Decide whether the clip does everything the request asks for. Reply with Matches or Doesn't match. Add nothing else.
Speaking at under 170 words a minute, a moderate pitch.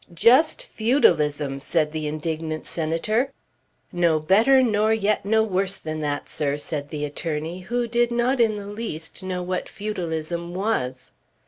Matches